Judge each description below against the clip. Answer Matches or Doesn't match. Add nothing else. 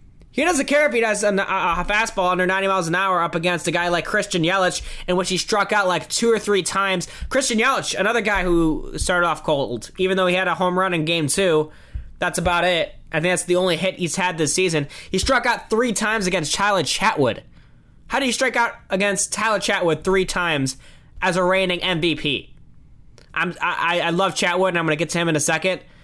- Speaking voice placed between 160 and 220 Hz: Matches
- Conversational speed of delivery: Doesn't match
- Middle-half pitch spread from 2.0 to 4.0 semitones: Matches